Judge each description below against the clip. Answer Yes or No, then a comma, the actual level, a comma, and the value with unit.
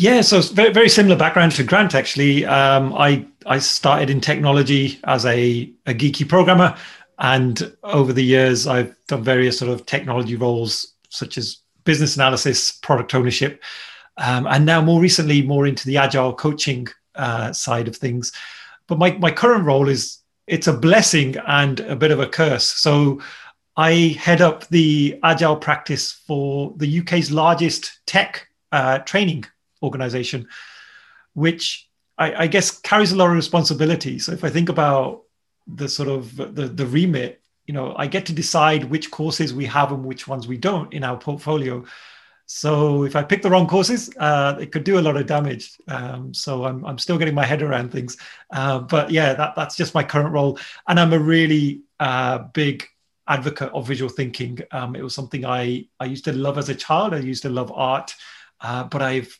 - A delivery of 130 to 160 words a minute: No, average, 185 wpm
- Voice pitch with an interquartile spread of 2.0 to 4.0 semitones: Yes, average, 3.5 semitones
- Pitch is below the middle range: No, medium, 145 Hz